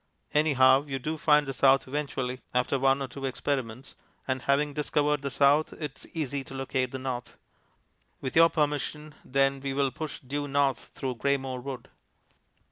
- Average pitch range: No, narrow, 1.9 semitones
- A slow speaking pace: No, average, 175 wpm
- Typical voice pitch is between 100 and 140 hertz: Yes, low, 135 Hz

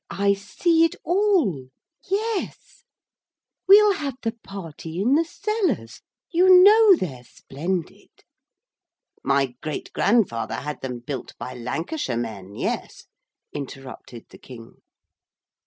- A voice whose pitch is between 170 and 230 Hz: Yes, high, 190 Hz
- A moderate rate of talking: No, slow, 110 wpm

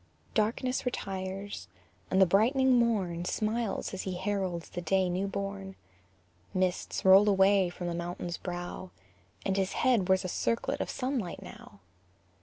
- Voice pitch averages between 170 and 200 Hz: Yes, high, 190 Hz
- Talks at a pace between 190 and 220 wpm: No, average, 150 wpm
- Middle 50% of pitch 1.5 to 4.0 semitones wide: Yes, average, 2.7 semitones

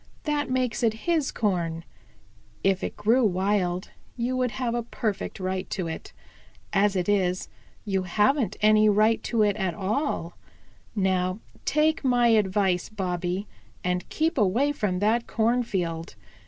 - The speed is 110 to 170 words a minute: Yes, average, 140 wpm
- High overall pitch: Yes, high, 210 Hz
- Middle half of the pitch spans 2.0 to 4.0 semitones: No, average, 4.4 semitones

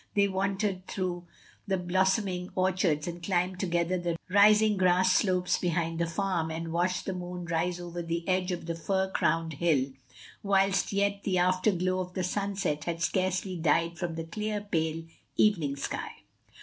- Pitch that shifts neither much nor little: No, narrow, 2.2 semitones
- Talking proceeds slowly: No, average, 160 wpm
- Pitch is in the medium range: Yes, medium, 180 Hz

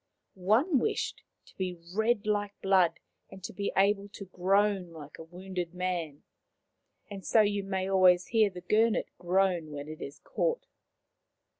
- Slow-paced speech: No, average, 155 wpm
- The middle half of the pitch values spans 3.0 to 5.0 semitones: No, narrow, 2.5 semitones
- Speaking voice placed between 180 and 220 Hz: Yes, high, 190 Hz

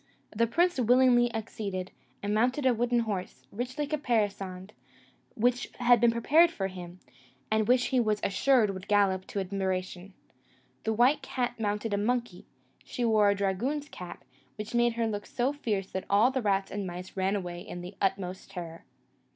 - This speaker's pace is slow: No, average, 175 wpm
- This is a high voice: Yes, high, 215 Hz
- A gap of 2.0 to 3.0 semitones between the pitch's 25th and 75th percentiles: No, average, 4.1 semitones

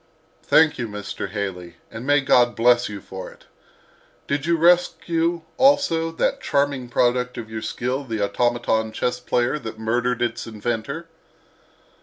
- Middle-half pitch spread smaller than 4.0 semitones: No, average, 4.5 semitones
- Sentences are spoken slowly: No, average, 145 wpm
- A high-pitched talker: No, low, 120 Hz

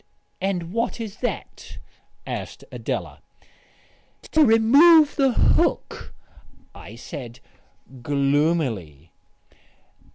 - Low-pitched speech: No, medium, 170 Hz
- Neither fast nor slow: No, slow, 75 wpm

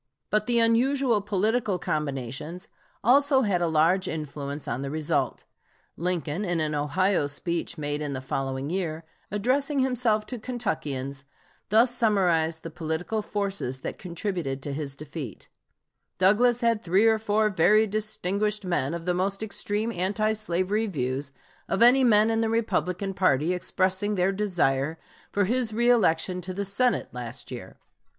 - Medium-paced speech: Yes, average, 150 wpm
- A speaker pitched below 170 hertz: No, medium, 185 Hz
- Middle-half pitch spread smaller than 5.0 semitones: No, wide, 5.6 semitones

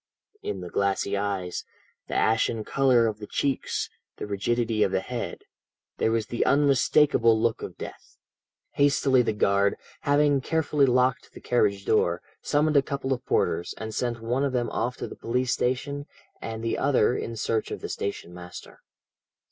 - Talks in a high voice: No, low, 115 Hz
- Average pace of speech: Yes, average, 170 wpm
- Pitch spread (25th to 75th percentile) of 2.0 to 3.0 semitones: No, average, 4.4 semitones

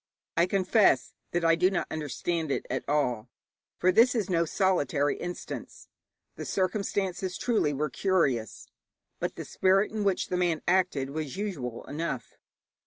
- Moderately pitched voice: Yes, medium, 175 Hz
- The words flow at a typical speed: Yes, average, 150 wpm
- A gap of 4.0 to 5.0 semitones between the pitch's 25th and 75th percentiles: Yes, average, 4.6 semitones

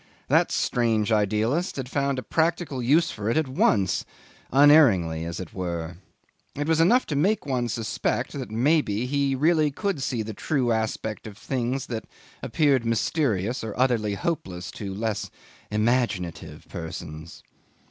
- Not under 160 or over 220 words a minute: No, average, 145 wpm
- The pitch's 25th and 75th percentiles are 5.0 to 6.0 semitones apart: Yes, average, 5.3 semitones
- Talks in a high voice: No, low, 120 Hz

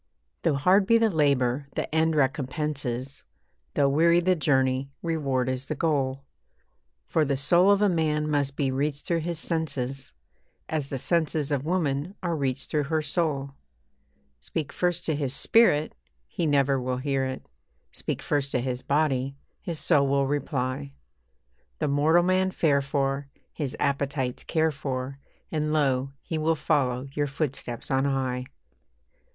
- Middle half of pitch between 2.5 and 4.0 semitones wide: Yes, average, 2.9 semitones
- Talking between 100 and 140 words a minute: No, average, 155 wpm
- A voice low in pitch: No, medium, 145 Hz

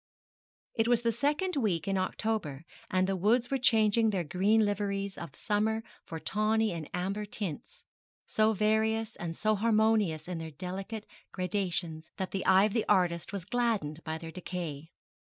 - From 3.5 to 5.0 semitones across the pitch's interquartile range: Yes, average, 3.8 semitones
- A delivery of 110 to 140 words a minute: No, average, 165 wpm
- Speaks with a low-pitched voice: No, high, 200 Hz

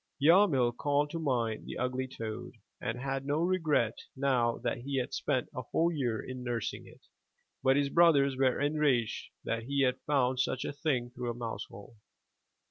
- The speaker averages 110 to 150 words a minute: No, average, 175 wpm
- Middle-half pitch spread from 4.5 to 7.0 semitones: No, average, 3.0 semitones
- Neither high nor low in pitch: No, low, 130 Hz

